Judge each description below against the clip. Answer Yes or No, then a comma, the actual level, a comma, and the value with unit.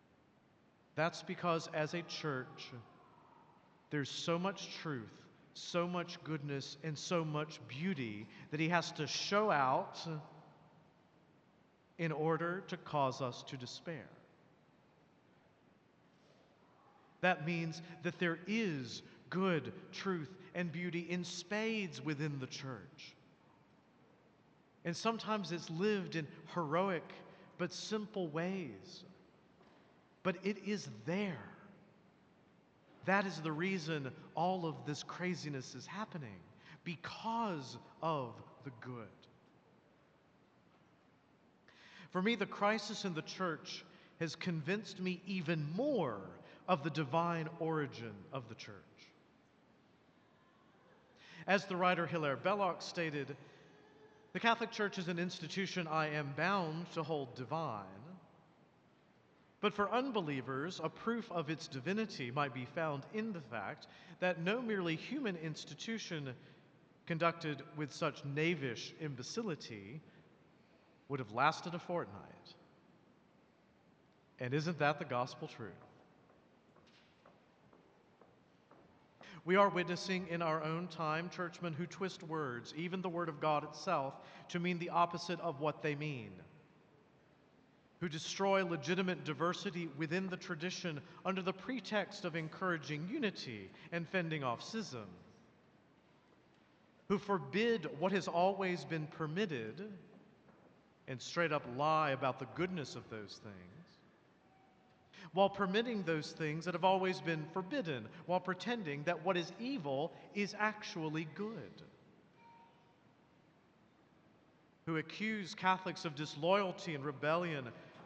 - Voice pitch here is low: No, medium, 170 Hz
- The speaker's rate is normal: No, slow, 115 wpm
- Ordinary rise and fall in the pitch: Yes, average, 3.6 semitones